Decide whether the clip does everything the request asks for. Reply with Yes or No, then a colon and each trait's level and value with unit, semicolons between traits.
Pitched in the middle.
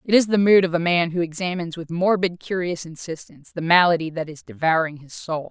Yes: medium, 170 Hz